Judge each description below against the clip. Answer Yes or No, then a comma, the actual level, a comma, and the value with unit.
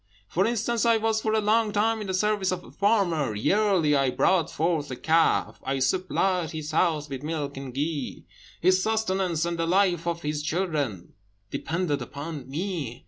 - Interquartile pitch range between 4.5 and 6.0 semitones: Yes, average, 5.1 semitones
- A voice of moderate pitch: Yes, medium, 170 Hz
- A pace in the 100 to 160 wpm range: No, average, 180 wpm